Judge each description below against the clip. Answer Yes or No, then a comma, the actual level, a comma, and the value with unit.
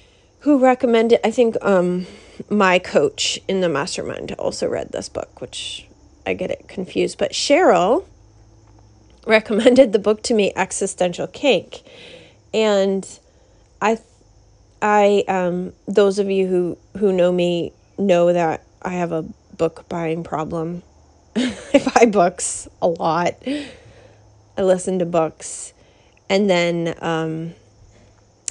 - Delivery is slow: Yes, slow, 125 wpm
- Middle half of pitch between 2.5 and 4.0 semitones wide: No, average, 4.7 semitones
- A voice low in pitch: No, medium, 185 Hz